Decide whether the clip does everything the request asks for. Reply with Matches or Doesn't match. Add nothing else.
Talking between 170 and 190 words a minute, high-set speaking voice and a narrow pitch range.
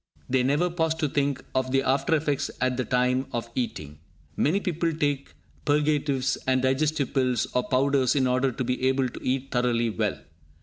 Doesn't match